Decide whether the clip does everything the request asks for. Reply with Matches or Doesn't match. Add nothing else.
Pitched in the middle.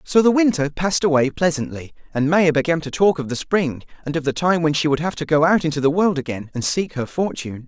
Matches